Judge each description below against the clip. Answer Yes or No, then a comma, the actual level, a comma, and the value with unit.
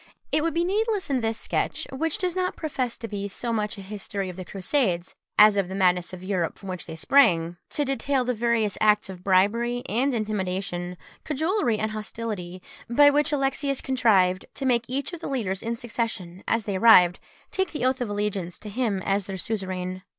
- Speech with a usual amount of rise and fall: No, wide, 5.8 semitones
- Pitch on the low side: No, high, 215 Hz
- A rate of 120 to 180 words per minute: No, average, 200 wpm